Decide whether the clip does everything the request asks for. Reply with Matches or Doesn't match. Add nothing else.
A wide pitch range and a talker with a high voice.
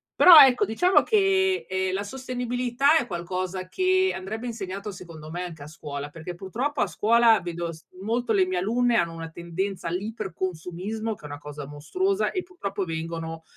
Matches